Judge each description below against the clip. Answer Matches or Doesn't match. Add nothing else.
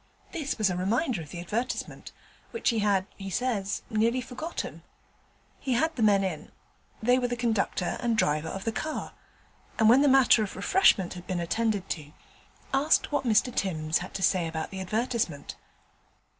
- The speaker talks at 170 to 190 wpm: Matches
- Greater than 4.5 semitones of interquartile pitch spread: Matches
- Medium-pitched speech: Doesn't match